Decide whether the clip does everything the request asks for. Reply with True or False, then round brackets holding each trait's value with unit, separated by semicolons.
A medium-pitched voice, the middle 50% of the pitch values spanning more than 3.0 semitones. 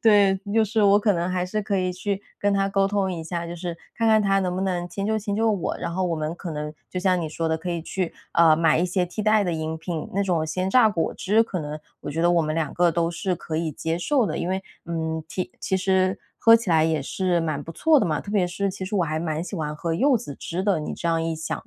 True (180 Hz; 3.4 semitones)